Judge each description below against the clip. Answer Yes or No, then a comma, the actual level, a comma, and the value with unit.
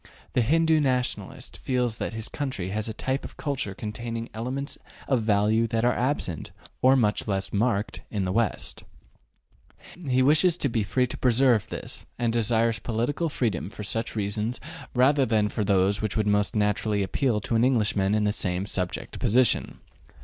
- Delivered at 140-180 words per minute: Yes, average, 170 wpm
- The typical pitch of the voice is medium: No, low, 115 Hz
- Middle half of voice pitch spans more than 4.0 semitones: No, average, 3.5 semitones